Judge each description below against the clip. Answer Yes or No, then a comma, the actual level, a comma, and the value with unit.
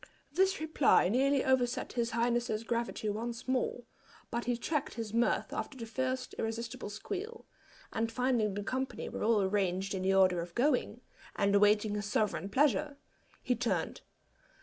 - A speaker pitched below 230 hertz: No, high, 235 Hz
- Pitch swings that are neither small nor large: Yes, average, 3.8 semitones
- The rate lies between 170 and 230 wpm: No, average, 155 wpm